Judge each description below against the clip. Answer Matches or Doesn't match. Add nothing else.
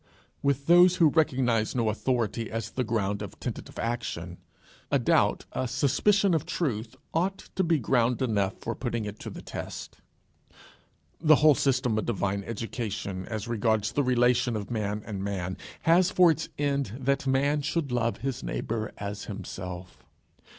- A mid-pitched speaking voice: Doesn't match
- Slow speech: Doesn't match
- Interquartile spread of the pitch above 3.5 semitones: Matches